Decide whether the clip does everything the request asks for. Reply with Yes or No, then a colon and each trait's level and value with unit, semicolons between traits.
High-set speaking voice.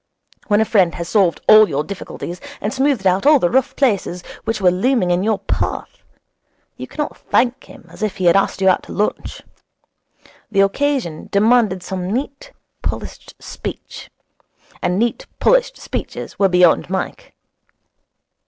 Yes: high, 200 Hz